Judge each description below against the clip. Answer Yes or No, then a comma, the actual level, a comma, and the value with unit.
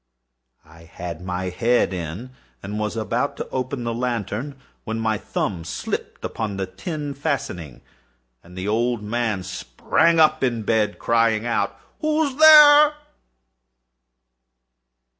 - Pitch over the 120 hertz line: No, low, 115 Hz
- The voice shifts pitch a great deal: Yes, wide, 5.7 semitones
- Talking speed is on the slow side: Yes, slow, 120 wpm